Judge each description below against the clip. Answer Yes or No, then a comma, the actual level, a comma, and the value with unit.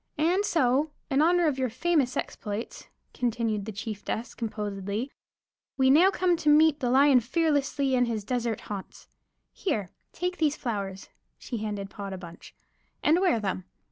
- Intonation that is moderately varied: No, wide, 6.4 semitones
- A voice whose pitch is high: Yes, very high, 250 Hz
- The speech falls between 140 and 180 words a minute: Yes, average, 155 wpm